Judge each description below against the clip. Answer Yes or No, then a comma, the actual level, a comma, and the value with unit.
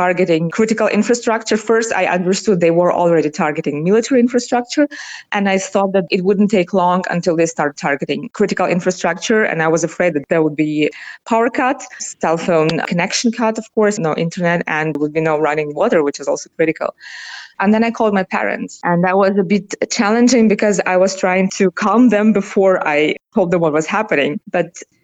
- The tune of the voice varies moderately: Yes, average, 4.4 semitones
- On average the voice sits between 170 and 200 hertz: Yes, high, 190 Hz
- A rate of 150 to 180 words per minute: No, average, 195 wpm